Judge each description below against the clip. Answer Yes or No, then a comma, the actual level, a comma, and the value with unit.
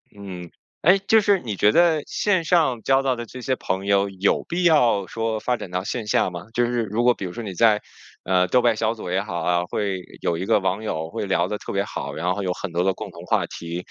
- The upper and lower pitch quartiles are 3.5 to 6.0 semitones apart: Yes, average, 5.0 semitones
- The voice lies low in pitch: Yes, low, 105 Hz